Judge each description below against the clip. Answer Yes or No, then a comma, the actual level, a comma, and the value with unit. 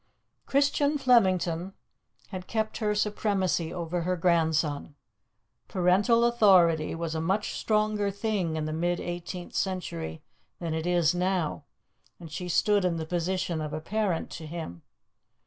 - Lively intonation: No, average, 3.9 semitones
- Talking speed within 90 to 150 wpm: Yes, average, 140 wpm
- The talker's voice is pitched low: No, medium, 180 Hz